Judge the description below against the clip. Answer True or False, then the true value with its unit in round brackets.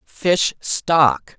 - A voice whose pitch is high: False (155 Hz)